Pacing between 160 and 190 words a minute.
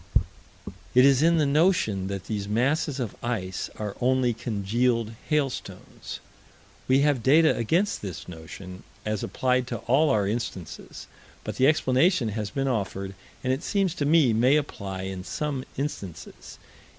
No: average, 150 wpm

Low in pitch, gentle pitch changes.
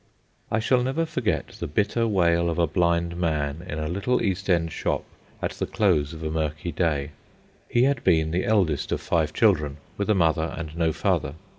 No: very low, 85 Hz; average, 4.2 semitones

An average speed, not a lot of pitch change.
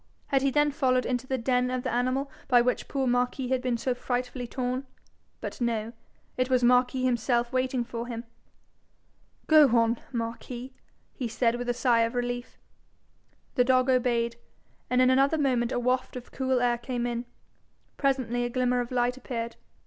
Yes: average, 175 wpm; narrow, 1.3 semitones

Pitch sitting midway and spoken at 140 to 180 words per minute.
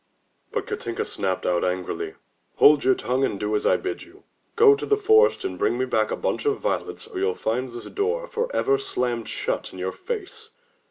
No: medium, 150 Hz; fast, 205 wpm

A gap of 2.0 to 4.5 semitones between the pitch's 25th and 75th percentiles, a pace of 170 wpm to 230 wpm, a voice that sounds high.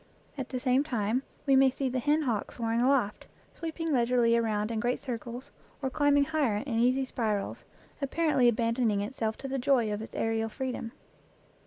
Yes: average, 3.1 semitones; average, 180 wpm; very high, 250 Hz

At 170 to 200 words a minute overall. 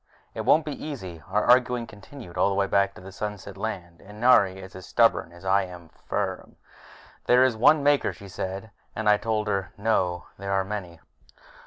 Yes: average, 195 wpm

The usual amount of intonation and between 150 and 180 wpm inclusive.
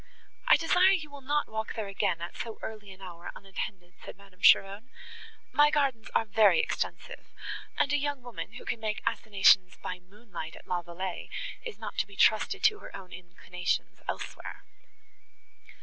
No: wide, 6.7 semitones; average, 170 wpm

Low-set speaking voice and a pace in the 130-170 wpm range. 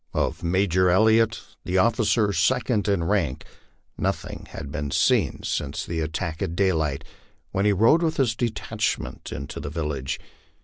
Yes: very low, 90 Hz; average, 150 wpm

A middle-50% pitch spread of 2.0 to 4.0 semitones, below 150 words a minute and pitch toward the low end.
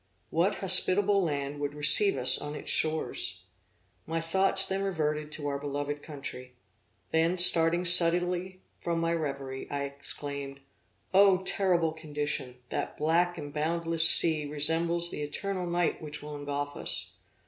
No: average, 3.3 semitones; average, 140 wpm; medium, 160 Hz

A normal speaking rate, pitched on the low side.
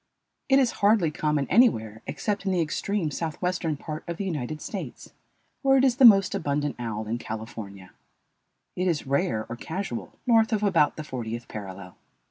No: average, 170 wpm; medium, 155 Hz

